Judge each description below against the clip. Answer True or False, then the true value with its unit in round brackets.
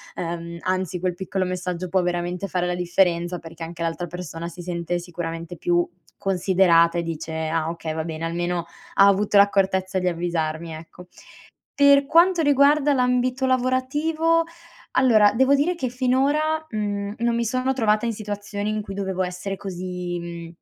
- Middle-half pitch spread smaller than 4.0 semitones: False (6.0 semitones)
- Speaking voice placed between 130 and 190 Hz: True (185 Hz)